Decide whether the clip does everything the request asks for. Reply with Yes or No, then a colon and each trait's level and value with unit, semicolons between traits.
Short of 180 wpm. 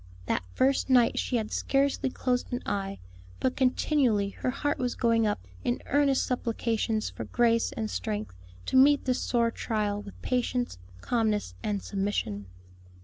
Yes: average, 150 wpm